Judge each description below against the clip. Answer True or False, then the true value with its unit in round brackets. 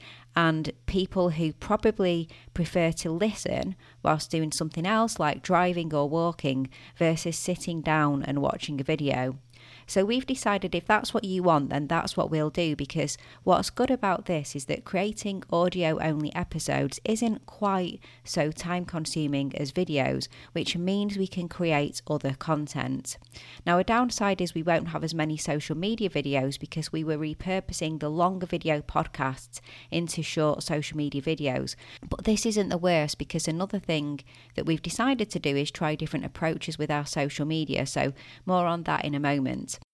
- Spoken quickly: False (170 wpm)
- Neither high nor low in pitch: True (160 Hz)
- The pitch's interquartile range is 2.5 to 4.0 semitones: True (3.7 semitones)